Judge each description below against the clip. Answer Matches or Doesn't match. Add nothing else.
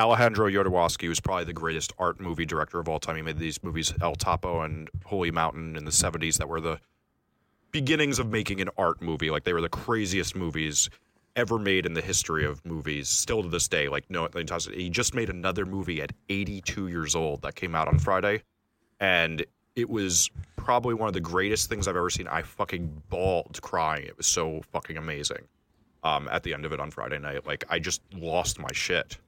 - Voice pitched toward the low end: Matches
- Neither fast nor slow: Doesn't match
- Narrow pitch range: Doesn't match